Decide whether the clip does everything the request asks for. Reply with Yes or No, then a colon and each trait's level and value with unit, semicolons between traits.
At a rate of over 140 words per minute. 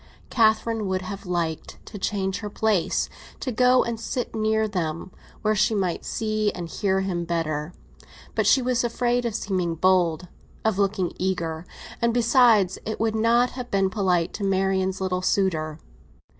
Yes: average, 155 wpm